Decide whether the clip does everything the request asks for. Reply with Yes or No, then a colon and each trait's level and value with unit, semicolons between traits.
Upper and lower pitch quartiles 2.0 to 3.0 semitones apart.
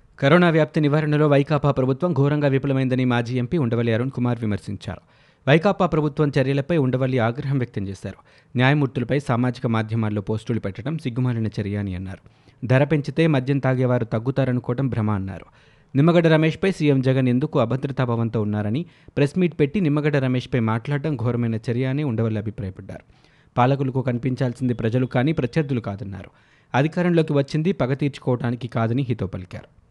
No: average, 4.0 semitones